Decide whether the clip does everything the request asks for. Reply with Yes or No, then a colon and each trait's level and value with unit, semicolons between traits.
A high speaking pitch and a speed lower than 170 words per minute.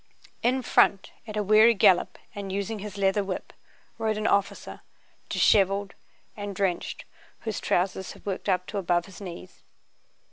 Yes: high, 200 Hz; average, 150 wpm